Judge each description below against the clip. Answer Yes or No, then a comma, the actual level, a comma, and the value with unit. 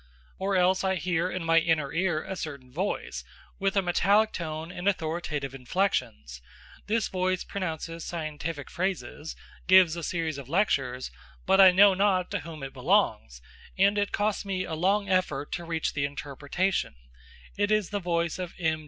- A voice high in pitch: No, medium, 175 Hz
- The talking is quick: No, average, 170 wpm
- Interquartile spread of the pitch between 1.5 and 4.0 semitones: Yes, average, 3.6 semitones